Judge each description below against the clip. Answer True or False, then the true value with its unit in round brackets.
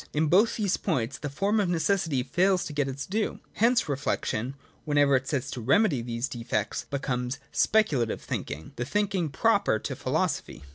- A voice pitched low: False (145 Hz)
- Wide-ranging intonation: True (7.5 semitones)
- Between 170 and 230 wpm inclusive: True (175 wpm)